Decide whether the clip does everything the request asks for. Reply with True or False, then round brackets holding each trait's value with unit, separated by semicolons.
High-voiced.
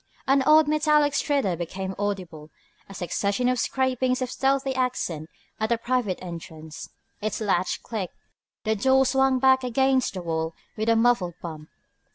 True (230 Hz)